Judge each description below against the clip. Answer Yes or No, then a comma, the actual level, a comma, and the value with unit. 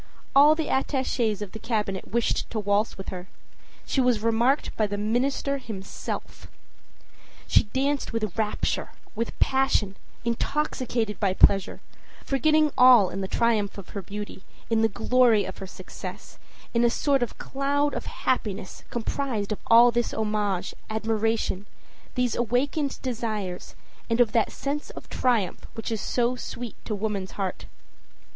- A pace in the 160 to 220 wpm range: No, average, 150 wpm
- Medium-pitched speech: No, high, 225 Hz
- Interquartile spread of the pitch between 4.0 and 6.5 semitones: No, average, 3.6 semitones